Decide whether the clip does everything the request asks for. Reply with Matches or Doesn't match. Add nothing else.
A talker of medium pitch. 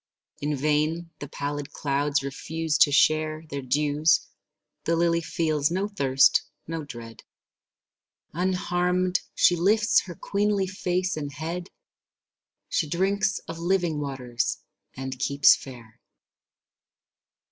Matches